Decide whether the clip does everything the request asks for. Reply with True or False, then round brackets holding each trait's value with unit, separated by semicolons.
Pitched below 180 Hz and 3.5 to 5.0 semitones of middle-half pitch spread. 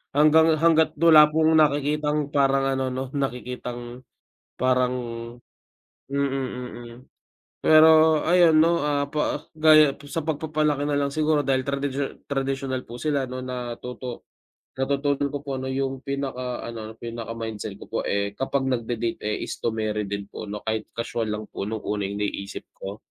True (135 Hz; 4.1 semitones)